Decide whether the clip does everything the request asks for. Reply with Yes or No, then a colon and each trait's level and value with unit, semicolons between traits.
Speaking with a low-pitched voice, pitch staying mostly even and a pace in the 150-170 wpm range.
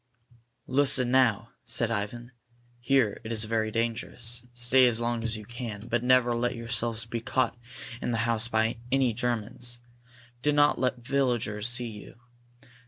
Yes: low, 120 Hz; narrow, 1.5 semitones; average, 160 wpm